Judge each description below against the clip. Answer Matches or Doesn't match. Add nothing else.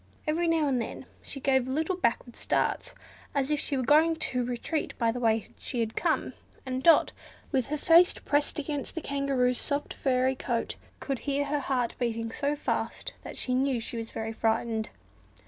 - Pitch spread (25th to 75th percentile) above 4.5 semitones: Doesn't match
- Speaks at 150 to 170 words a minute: Doesn't match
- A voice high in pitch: Matches